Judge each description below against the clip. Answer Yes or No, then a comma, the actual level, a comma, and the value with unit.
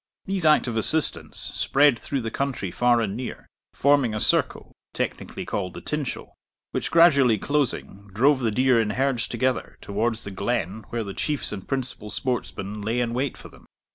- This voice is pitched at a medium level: No, low, 120 Hz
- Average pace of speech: Yes, average, 170 wpm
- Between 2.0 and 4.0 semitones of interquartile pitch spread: No, average, 4.4 semitones